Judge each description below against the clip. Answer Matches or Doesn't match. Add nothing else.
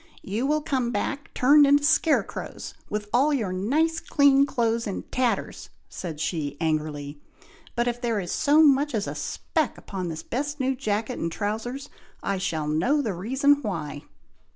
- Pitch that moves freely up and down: Matches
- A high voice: Matches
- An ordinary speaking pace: Matches